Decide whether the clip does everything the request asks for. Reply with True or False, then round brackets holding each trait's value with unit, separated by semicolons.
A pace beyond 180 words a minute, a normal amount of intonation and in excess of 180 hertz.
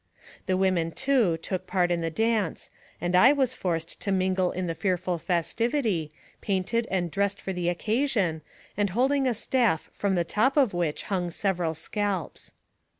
False (165 wpm; 4.4 semitones; 190 Hz)